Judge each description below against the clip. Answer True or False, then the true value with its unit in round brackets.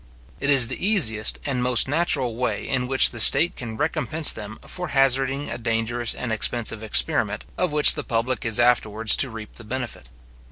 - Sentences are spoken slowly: False (185 wpm)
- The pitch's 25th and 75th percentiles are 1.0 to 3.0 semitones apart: False (3.7 semitones)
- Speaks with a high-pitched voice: False (125 Hz)